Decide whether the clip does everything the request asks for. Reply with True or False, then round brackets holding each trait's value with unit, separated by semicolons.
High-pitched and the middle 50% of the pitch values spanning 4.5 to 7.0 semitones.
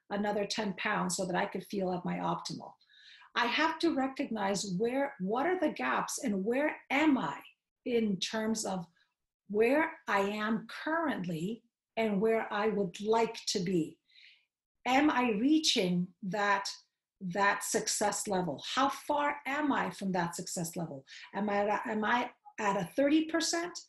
True (220 Hz; 5.5 semitones)